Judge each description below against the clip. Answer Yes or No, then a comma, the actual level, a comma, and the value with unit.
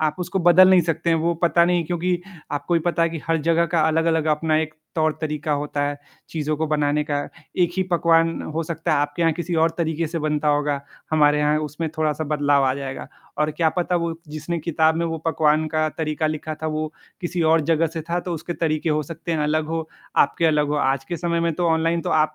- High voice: No, medium, 160 Hz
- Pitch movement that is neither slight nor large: No, narrow, 1.8 semitones